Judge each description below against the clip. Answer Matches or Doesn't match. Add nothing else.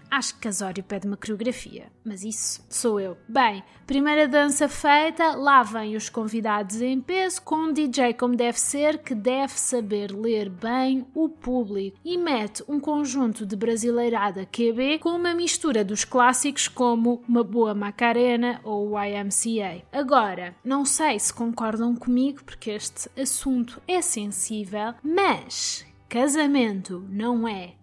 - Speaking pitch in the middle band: Doesn't match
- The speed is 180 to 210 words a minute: Doesn't match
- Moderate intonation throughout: Matches